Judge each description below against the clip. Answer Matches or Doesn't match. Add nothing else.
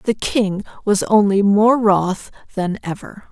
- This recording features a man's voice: Doesn't match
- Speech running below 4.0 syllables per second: Matches